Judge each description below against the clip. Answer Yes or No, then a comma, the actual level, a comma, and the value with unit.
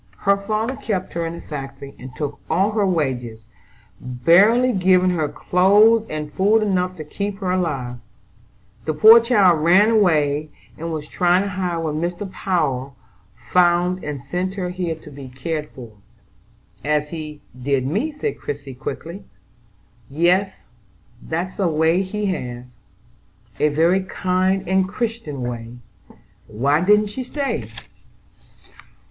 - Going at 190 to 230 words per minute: No, average, 140 wpm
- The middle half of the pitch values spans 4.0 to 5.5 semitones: Yes, average, 4.8 semitones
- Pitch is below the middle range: No, medium, 175 Hz